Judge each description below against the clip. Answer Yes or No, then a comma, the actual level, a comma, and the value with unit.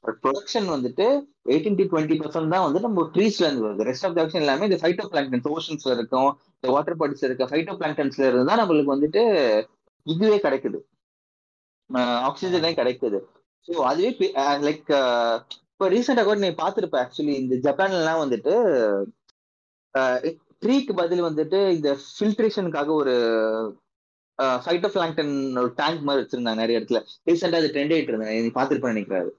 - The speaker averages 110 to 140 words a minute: Yes, average, 120 wpm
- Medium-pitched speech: Yes, medium, 150 Hz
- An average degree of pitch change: No, wide, 5.9 semitones